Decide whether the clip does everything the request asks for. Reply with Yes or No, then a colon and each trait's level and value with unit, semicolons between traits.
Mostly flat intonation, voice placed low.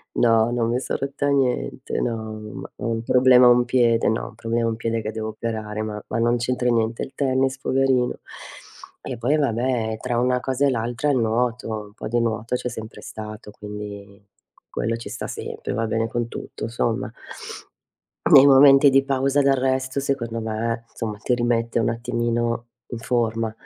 Yes: narrow, 2.3 semitones; low, 120 Hz